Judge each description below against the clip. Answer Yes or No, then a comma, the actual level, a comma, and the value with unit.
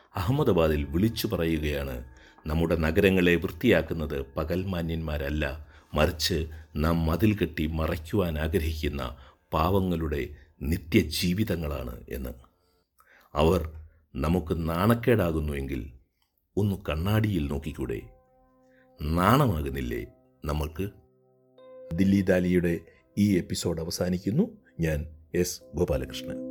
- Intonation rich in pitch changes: No, average, 3.9 semitones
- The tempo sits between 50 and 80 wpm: Yes, average, 70 wpm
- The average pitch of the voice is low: Yes, very low, 85 Hz